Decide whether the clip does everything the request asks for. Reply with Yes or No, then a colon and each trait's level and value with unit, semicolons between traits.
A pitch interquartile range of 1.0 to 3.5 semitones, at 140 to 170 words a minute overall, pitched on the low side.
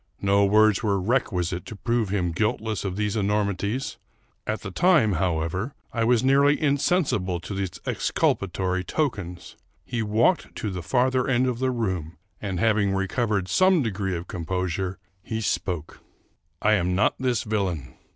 No: average, 4.4 semitones; average, 165 wpm; low, 105 Hz